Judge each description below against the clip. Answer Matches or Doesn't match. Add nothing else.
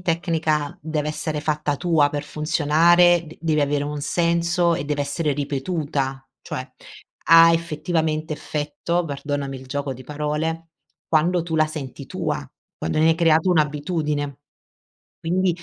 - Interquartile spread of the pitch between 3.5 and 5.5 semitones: Doesn't match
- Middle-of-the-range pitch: Matches